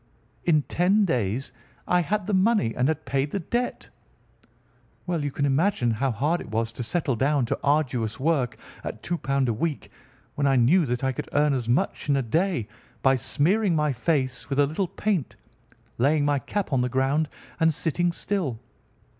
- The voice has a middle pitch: Yes, medium, 145 Hz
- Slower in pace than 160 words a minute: No, average, 190 wpm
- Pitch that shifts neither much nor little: Yes, average, 4.9 semitones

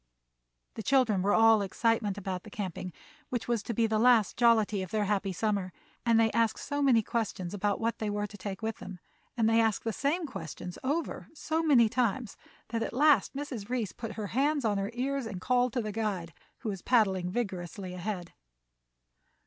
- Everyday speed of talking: Yes, average, 195 wpm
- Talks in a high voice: Yes, high, 220 Hz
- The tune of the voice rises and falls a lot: No, average, 3.4 semitones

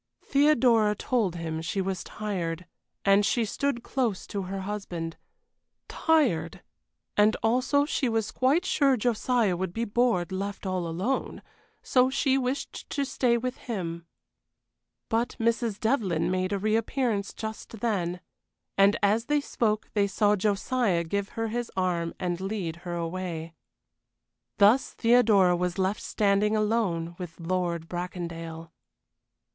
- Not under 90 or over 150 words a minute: Yes, slow, 135 wpm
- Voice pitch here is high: Yes, high, 205 Hz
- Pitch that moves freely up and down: No, average, 4.8 semitones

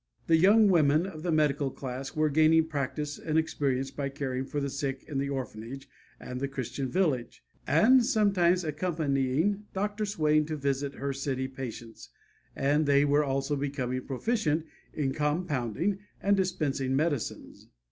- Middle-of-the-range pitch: Yes, medium, 145 Hz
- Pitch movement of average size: Yes, average, 3.2 semitones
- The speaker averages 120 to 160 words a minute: Yes, average, 150 wpm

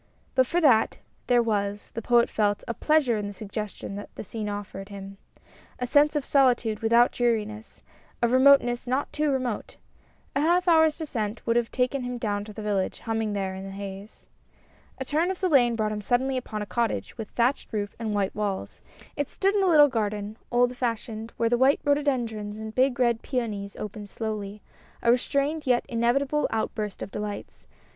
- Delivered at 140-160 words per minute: No, average, 190 wpm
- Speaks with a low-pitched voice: No, high, 230 Hz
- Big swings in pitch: No, average, 3.9 semitones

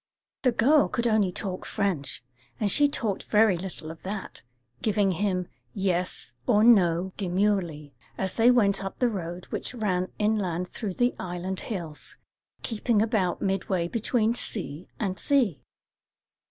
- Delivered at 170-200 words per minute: No, average, 140 wpm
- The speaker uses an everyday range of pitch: Yes, average, 3.5 semitones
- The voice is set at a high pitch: Yes, high, 195 Hz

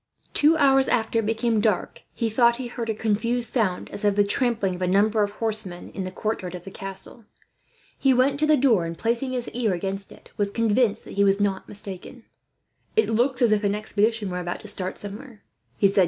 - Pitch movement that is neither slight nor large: Yes, average, 3.3 semitones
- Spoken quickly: Yes, fast, 220 wpm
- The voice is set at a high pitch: Yes, high, 215 Hz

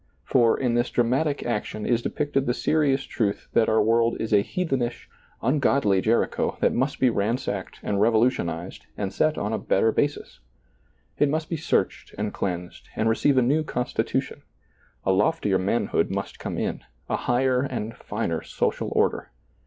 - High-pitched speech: No, low, 120 Hz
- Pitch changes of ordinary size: Yes, average, 4.5 semitones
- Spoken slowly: No, average, 160 wpm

